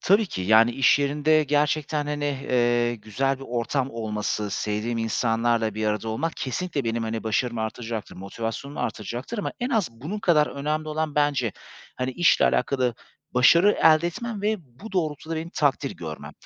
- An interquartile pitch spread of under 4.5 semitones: No, wide, 5.5 semitones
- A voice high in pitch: No, low, 135 Hz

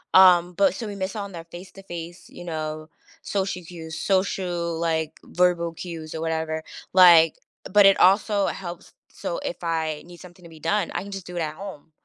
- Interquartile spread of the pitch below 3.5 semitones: Yes, narrow, 2.6 semitones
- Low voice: No, medium, 175 Hz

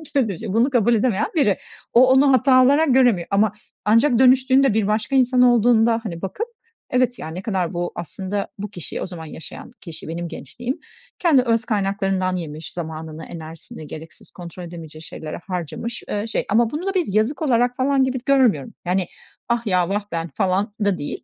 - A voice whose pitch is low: No, high, 210 Hz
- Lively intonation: Yes, wide, 6.2 semitones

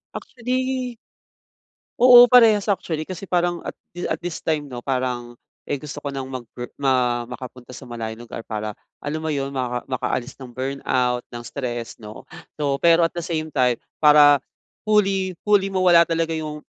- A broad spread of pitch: Yes, wide, 5.9 semitones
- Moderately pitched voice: Yes, medium, 145 Hz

